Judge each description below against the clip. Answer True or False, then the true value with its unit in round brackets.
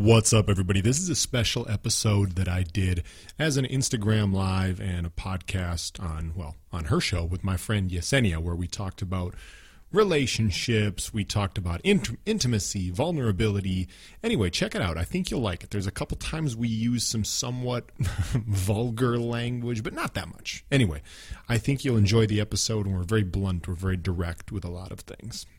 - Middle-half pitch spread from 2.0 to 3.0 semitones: False (4.3 semitones)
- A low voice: True (105 Hz)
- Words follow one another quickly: False (190 wpm)